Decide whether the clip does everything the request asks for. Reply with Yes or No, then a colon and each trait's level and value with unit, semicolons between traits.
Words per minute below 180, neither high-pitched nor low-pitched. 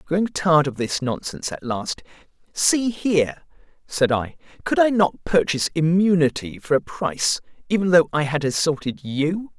Yes: average, 155 wpm; medium, 165 Hz